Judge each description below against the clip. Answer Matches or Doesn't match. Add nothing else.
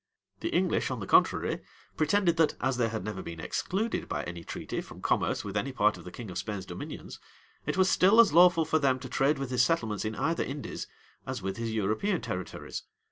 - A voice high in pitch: Doesn't match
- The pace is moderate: Doesn't match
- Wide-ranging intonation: Matches